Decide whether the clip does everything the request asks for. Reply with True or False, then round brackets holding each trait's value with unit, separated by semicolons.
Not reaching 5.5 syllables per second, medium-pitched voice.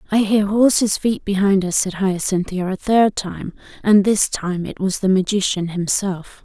False (4.4 syllables/s; 195 Hz)